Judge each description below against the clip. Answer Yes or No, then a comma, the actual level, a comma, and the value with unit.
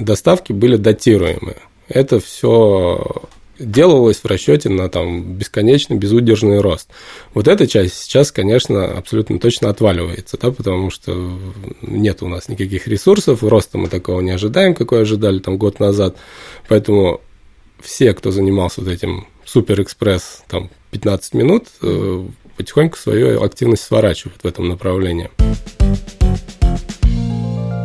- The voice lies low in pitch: Yes, low, 100 Hz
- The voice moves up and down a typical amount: Yes, average, 3.3 semitones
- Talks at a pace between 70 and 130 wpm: Yes, average, 120 wpm